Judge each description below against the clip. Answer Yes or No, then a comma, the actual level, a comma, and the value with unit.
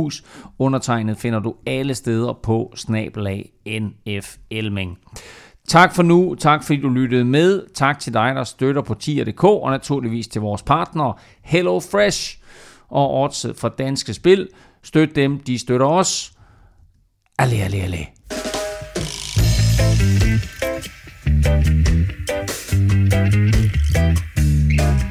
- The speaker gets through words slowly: Yes, slow, 100 wpm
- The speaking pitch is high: No, low, 115 Hz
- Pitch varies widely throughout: Yes, wide, 5.9 semitones